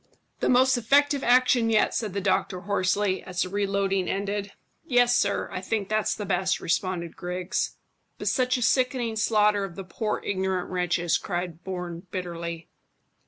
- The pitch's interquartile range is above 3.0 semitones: Yes, average, 3.5 semitones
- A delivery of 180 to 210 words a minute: No, average, 155 wpm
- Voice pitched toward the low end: No, high, 195 Hz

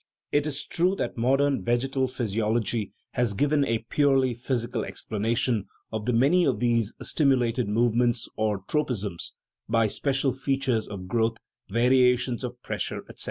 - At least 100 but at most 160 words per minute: Yes, average, 140 wpm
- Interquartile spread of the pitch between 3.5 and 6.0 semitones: No, average, 3.1 semitones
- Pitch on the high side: No, low, 120 Hz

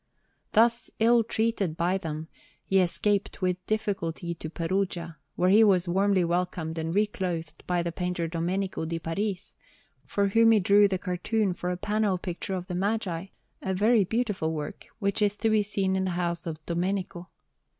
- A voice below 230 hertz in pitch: Yes, medium, 185 Hz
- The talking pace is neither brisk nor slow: Yes, average, 170 wpm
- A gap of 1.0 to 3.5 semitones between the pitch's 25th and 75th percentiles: Yes, average, 3.1 semitones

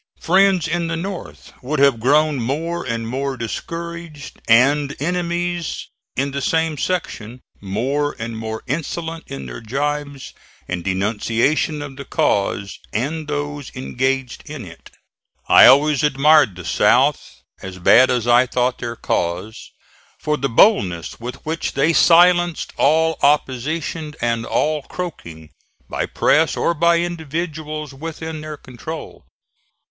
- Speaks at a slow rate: Yes, slow, 130 wpm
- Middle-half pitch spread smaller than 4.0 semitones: No, average, 5.2 semitones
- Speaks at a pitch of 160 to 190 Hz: No, medium, 145 Hz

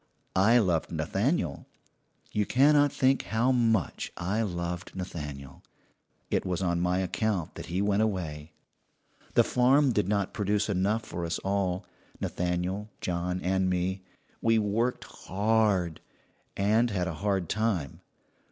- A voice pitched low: Yes, very low, 95 Hz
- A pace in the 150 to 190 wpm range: No, slow, 135 wpm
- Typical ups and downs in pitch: Yes, average, 3.8 semitones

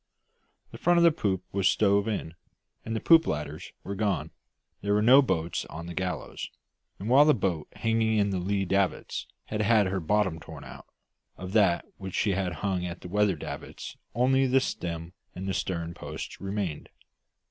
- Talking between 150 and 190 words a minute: Yes, average, 180 wpm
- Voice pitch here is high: No, low, 100 Hz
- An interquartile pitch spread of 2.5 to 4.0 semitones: Yes, average, 3.7 semitones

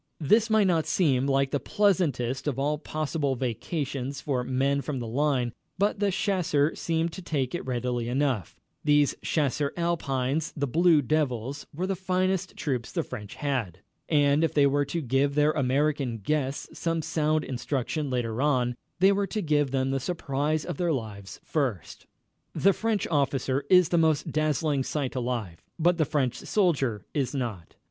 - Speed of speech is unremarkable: Yes, average, 170 wpm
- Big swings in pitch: No, average, 3.9 semitones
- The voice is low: No, medium, 145 Hz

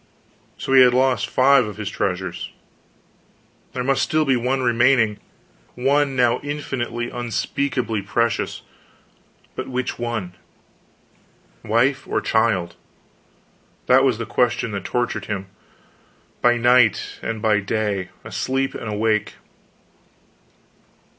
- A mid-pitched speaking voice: No, low, 120 Hz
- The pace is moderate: No, slow, 115 wpm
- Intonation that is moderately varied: Yes, average, 3.4 semitones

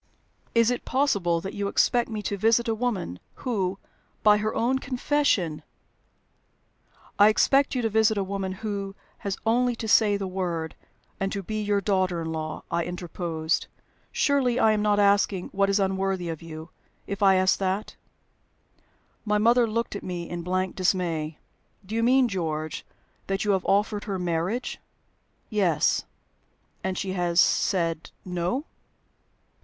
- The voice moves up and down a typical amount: Yes, average, 3.7 semitones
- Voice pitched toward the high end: Yes, high, 195 Hz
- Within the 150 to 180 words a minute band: Yes, average, 160 wpm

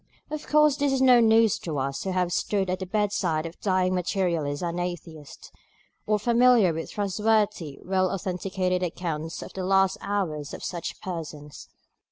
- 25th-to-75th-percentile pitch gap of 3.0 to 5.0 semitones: Yes, average, 3.7 semitones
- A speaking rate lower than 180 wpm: Yes, average, 170 wpm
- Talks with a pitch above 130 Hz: Yes, medium, 185 Hz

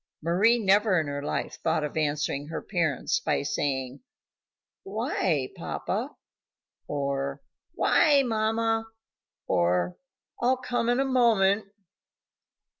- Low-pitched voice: No, medium, 185 Hz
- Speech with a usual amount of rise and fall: No, wide, 8.0 semitones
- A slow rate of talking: Yes, slow, 110 wpm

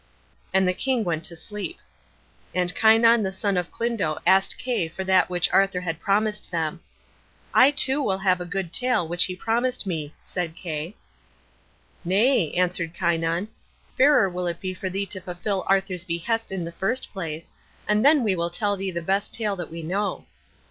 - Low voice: No, high, 190 Hz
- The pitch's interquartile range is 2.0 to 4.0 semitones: Yes, average, 3.4 semitones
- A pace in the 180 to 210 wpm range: Yes, average, 185 wpm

